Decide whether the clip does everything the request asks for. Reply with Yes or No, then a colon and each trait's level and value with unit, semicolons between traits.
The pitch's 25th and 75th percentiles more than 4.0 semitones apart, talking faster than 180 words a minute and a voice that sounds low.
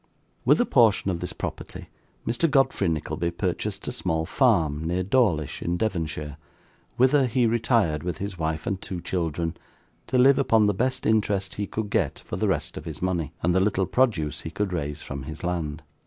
Yes: wide, 5.5 semitones; average, 190 wpm; very low, 90 Hz